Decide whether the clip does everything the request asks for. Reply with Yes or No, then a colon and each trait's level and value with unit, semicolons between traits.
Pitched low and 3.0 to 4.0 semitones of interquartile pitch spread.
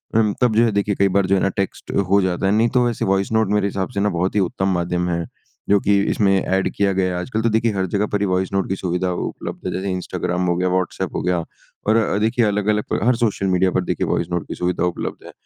No: very low, 95 Hz; narrow, 2.4 semitones